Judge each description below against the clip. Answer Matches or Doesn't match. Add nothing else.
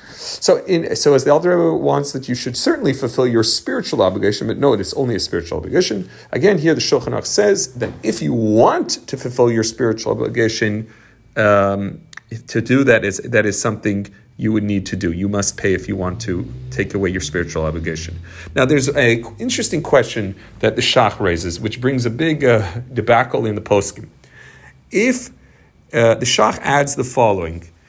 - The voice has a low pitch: Matches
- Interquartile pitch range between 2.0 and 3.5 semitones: Doesn't match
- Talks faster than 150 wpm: Matches